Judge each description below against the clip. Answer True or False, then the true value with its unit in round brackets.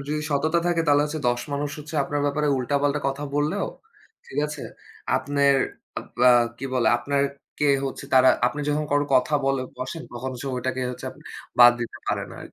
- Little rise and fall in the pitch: True (2.2 semitones)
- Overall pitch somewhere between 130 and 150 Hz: True (140 Hz)